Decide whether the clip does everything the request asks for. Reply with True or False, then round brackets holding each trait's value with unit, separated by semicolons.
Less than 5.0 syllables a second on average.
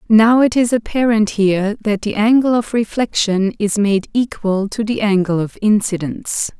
True (4.7 syllables/s)